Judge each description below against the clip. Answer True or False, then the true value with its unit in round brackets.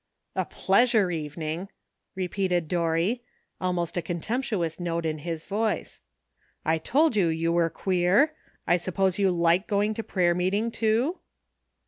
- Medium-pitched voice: True (180 Hz)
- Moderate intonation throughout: True (3.8 semitones)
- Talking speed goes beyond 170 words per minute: False (150 wpm)